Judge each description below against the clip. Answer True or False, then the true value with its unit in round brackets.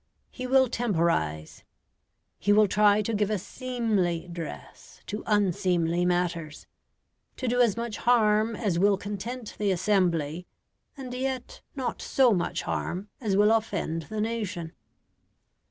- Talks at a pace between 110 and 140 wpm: True (135 wpm)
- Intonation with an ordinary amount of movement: True (4.6 semitones)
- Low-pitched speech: False (205 Hz)